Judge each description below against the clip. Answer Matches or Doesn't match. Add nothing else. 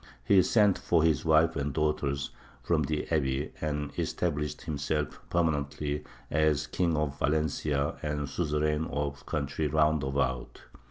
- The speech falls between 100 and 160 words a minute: Matches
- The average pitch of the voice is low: Matches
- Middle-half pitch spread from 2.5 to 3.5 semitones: Doesn't match